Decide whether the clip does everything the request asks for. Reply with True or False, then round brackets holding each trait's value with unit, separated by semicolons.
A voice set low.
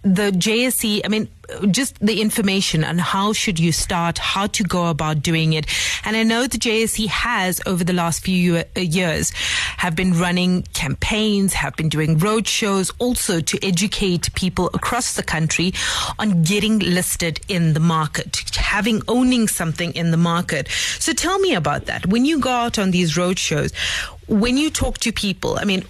False (190 Hz)